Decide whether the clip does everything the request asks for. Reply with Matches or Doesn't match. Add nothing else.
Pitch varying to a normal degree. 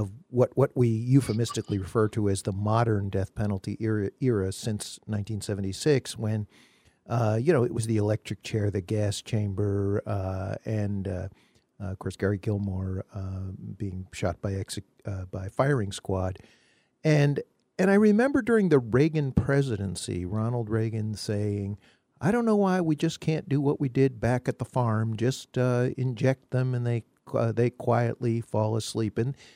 Matches